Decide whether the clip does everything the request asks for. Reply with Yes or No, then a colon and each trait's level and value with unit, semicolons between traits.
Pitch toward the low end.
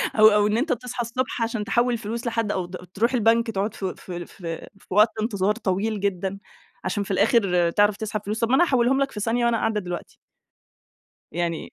No: high, 215 Hz